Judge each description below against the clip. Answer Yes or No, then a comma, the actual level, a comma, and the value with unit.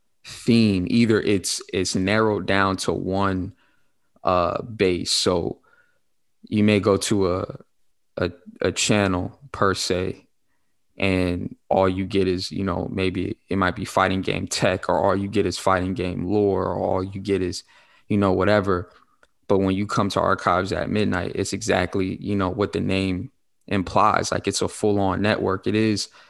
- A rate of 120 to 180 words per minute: Yes, average, 170 wpm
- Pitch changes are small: Yes, narrow, 1.6 semitones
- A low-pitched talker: Yes, very low, 95 Hz